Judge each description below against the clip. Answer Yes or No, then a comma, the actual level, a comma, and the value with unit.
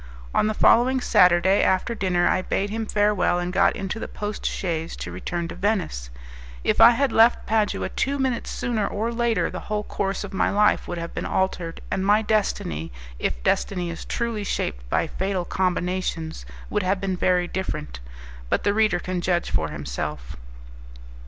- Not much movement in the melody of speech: No, average, 3.5 semitones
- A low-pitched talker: No, high, 190 Hz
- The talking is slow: No, average, 180 wpm